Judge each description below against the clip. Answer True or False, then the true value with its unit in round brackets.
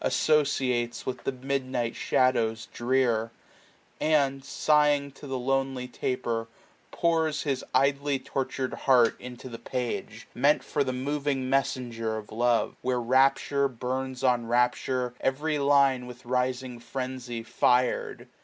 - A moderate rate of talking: False (125 wpm)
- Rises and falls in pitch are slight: True (2.0 semitones)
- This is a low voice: True (130 Hz)